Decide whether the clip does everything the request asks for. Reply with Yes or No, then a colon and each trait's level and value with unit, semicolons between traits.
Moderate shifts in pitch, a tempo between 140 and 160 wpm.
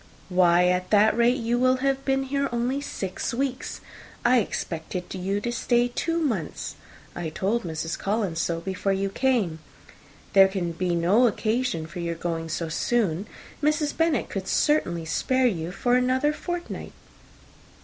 No: wide, 6.6 semitones; average, 155 wpm